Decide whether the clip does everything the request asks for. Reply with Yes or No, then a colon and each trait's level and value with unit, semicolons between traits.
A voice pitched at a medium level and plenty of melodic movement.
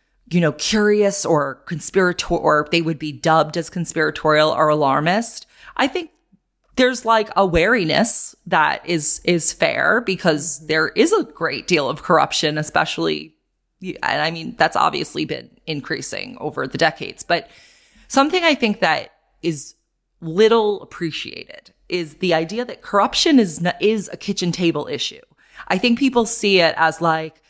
No: medium, 170 Hz; average, 5.0 semitones